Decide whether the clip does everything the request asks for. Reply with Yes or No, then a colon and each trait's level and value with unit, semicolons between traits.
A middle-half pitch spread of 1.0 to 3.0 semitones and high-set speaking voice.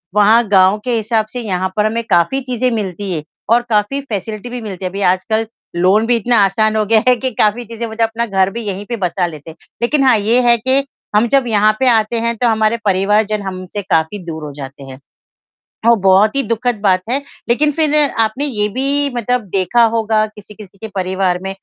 No: average, 3.6 semitones; high, 215 Hz